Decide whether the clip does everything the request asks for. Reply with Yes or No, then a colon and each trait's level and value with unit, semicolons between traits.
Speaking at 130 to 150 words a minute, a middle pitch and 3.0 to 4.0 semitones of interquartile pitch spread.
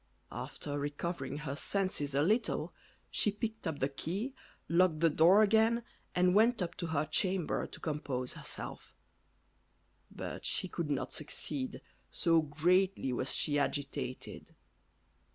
No: slow, 135 wpm; medium, 160 Hz; average, 4.8 semitones